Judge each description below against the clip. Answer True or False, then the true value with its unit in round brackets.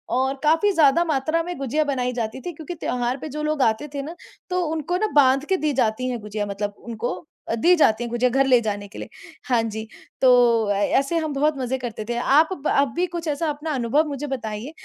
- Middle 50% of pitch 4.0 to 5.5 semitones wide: True (4.7 semitones)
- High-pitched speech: True (270 Hz)